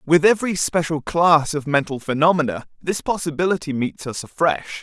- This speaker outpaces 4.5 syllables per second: Yes, 5.2 syllables/s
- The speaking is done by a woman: No, male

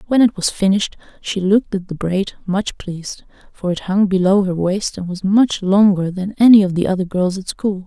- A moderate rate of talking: No, fast, 215 wpm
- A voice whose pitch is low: No, high, 190 Hz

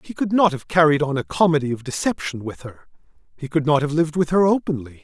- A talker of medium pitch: Yes, medium, 155 Hz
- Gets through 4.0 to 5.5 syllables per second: No, 6.3 syllables/s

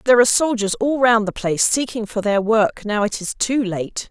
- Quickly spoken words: Yes, fast, 235 wpm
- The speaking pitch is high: Yes, high, 220 Hz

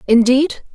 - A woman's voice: Yes, female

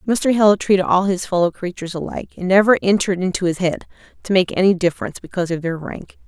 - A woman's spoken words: Yes, female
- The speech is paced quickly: Yes, fast, 210 wpm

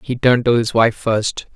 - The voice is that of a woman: No, male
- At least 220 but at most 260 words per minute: Yes, fast, 230 wpm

